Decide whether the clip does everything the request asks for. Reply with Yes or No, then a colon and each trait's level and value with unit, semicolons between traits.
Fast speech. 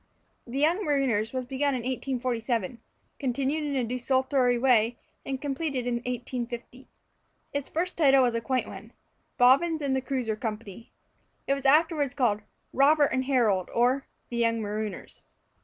No: average, 145 wpm